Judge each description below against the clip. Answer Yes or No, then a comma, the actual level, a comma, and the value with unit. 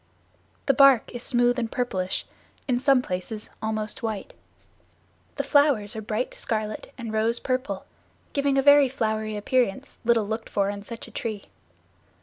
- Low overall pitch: No, high, 230 Hz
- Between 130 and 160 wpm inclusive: Yes, average, 150 wpm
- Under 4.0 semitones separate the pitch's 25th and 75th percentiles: Yes, average, 3.0 semitones